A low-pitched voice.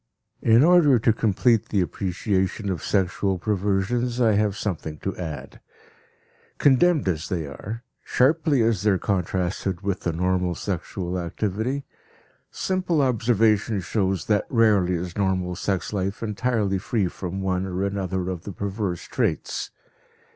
Yes: low, 100 Hz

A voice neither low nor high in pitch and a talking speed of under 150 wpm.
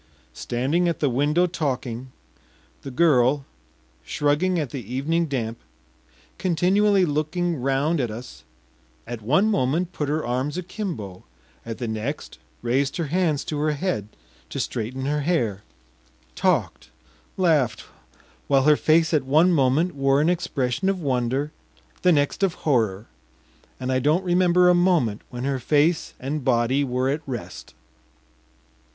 Yes: medium, 145 Hz; average, 140 wpm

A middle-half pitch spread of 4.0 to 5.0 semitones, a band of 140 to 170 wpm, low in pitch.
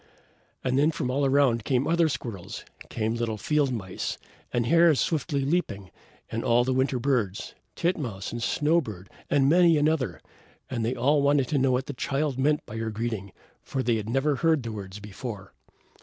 No: average, 4.3 semitones; average, 185 wpm; low, 130 Hz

